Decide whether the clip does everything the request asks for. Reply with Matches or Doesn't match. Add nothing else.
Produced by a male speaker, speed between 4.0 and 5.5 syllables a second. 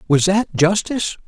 Matches